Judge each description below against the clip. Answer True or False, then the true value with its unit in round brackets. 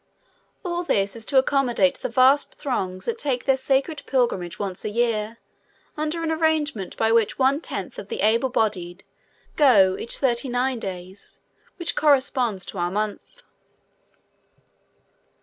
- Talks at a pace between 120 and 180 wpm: True (150 wpm)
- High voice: True (245 Hz)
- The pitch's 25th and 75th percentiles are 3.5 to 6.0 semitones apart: True (5.5 semitones)